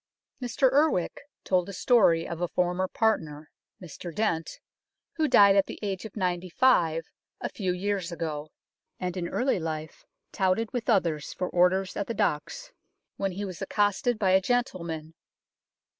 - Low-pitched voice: No, medium, 185 Hz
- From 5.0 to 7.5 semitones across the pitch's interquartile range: No, average, 3.8 semitones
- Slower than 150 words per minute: No, average, 160 wpm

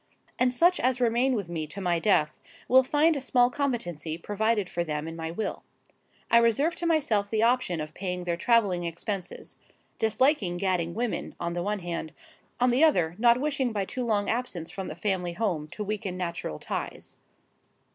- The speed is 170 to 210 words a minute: Yes, average, 180 wpm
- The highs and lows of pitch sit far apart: Yes, wide, 6.1 semitones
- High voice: Yes, high, 205 Hz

